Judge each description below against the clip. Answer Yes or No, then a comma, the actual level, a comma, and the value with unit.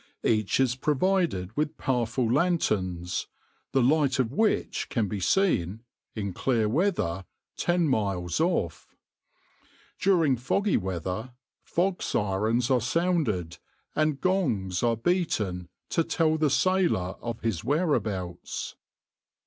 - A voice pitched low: Yes, low, 125 Hz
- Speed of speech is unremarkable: No, slow, 115 wpm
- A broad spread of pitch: Yes, wide, 8.9 semitones